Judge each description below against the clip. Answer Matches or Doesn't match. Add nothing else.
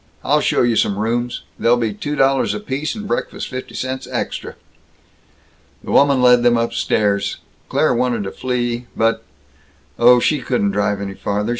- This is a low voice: Matches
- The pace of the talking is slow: Doesn't match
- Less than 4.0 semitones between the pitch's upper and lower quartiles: Matches